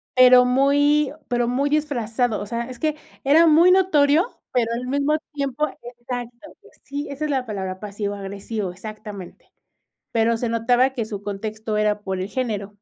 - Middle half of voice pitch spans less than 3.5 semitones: No, average, 4.8 semitones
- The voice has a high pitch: Yes, high, 240 Hz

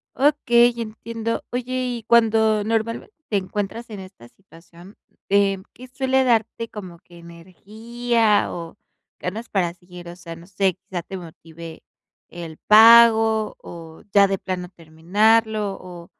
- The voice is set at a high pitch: Yes, high, 200 Hz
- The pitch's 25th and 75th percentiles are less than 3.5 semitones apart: No, average, 4.6 semitones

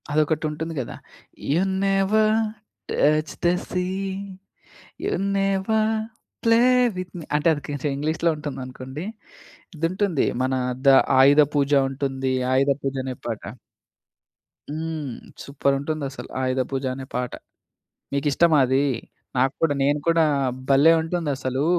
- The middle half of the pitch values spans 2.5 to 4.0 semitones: Yes, average, 3.6 semitones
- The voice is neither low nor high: Yes, medium, 150 Hz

